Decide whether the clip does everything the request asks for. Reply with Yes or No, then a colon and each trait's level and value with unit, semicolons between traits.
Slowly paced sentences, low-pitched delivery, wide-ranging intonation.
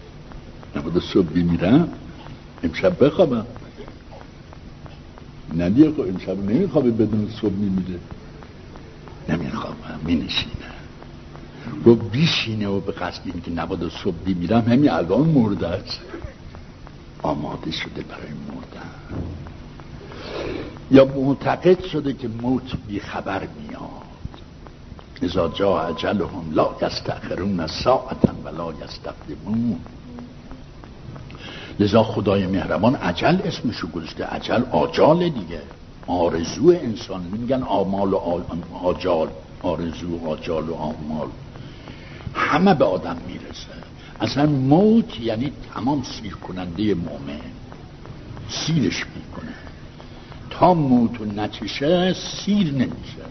Yes: slow, 95 wpm; low, 105 Hz; wide, 6.9 semitones